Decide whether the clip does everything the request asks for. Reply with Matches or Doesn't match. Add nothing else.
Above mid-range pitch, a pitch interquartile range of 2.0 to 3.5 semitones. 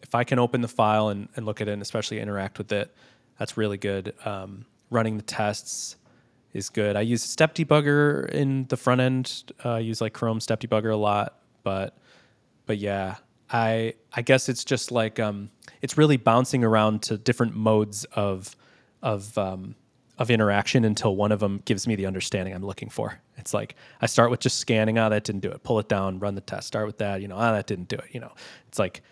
Doesn't match